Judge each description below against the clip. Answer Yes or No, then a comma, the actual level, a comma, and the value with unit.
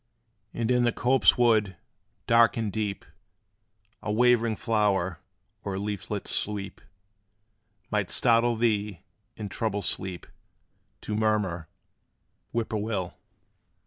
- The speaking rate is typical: No, slow, 110 wpm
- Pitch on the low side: Yes, low, 105 Hz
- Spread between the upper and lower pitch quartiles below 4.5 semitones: Yes, average, 2.8 semitones